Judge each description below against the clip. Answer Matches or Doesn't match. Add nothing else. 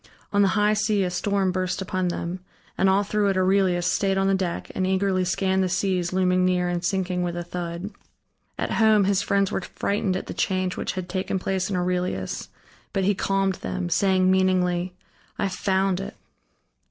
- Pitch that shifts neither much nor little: Doesn't match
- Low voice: Doesn't match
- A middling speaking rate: Matches